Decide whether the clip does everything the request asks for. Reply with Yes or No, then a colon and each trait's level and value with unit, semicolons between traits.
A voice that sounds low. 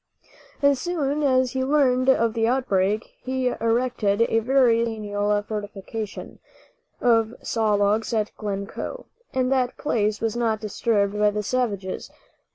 No: high, 225 Hz